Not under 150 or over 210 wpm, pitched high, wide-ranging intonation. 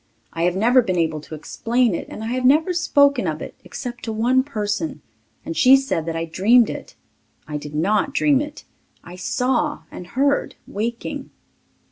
Yes: average, 180 wpm; high, 235 Hz; wide, 7.1 semitones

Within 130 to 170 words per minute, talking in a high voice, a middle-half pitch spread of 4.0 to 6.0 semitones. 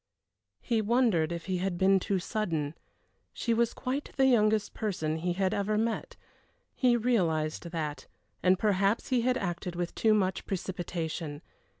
Yes: average, 155 wpm; high, 195 Hz; average, 4.4 semitones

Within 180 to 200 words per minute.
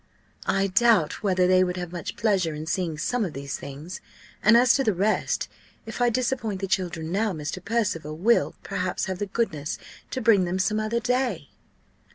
Yes: average, 190 wpm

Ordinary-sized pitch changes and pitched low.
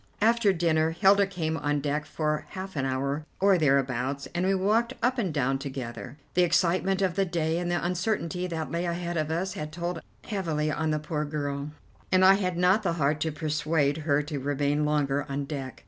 No: average, 3.9 semitones; medium, 160 Hz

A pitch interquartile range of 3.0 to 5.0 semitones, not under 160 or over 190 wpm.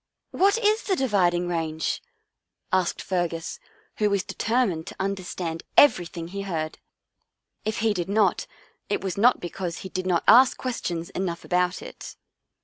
Yes: average, 4.0 semitones; average, 165 wpm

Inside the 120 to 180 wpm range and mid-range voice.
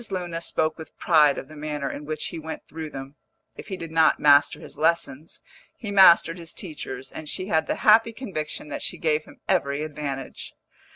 No: average, 195 wpm; medium, 155 Hz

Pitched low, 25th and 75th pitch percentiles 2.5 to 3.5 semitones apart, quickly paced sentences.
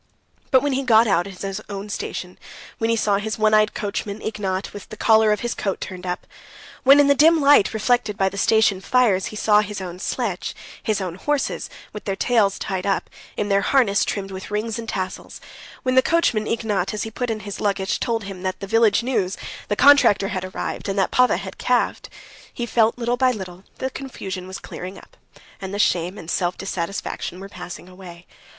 No: high, 205 Hz; average, 3.2 semitones; fast, 210 wpm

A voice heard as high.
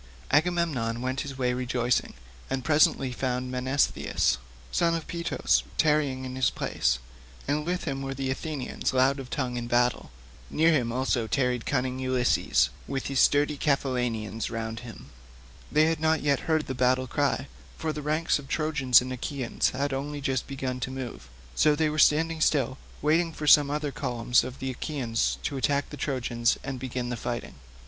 No: low, 135 Hz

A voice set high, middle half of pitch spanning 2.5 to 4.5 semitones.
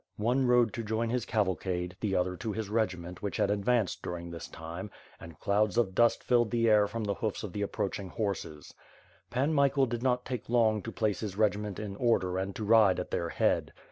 No: low, 105 Hz; average, 3.8 semitones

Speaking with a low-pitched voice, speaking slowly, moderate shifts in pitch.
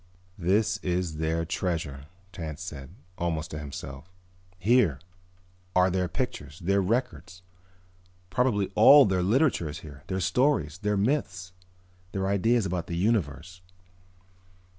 Yes: very low, 90 Hz; slow, 120 wpm; average, 4.1 semitones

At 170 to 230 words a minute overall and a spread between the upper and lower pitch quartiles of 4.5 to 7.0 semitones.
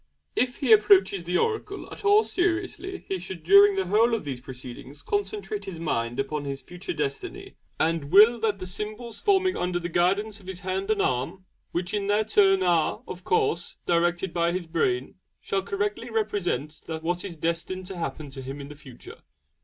Yes: average, 185 wpm; average, 5.0 semitones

